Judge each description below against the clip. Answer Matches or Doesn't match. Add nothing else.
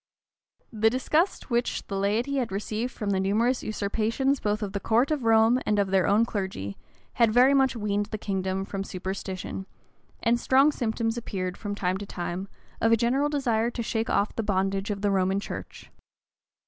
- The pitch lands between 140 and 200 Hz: Doesn't match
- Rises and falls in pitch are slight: Doesn't match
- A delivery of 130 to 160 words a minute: Doesn't match